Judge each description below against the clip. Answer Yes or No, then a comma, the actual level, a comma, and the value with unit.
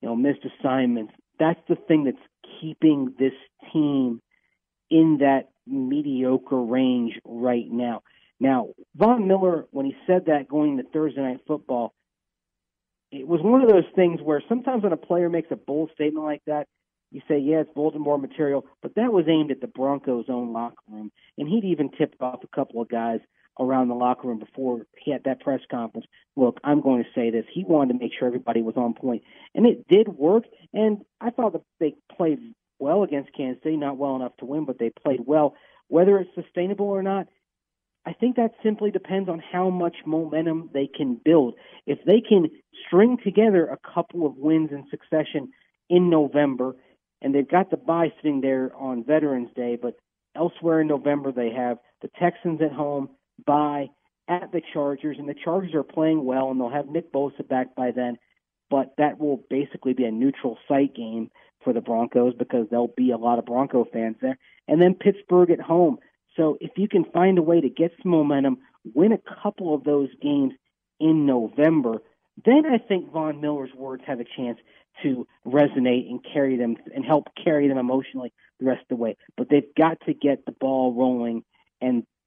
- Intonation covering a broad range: No, average, 4.8 semitones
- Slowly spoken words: No, average, 195 wpm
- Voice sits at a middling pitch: Yes, medium, 145 Hz